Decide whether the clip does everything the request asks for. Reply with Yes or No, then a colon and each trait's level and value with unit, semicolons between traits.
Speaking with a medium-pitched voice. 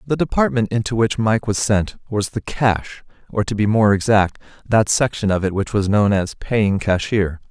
No: low, 105 Hz